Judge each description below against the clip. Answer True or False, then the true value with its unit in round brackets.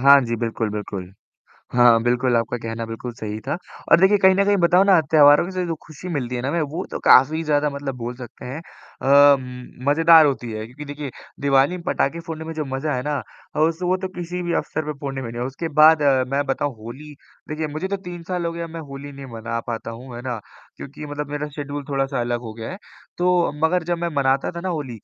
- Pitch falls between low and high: True (145 Hz)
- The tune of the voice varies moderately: True (5.0 semitones)